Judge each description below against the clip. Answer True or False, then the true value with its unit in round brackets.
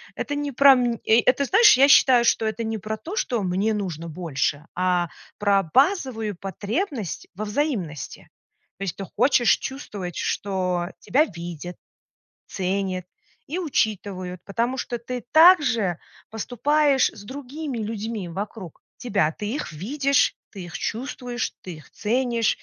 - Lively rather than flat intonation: True (6.0 semitones)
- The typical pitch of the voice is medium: False (220 Hz)